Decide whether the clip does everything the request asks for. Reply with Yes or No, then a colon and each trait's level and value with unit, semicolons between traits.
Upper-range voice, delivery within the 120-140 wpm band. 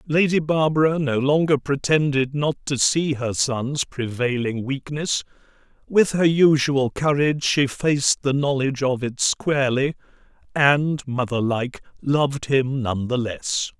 No: medium, 140 Hz; slow, 135 wpm